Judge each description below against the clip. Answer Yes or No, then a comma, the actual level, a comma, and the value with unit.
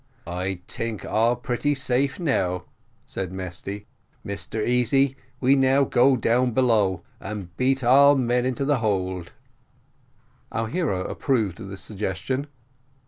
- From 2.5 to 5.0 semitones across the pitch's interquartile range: No, wide, 5.5 semitones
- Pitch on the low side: Yes, low, 115 Hz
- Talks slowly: Yes, slow, 130 wpm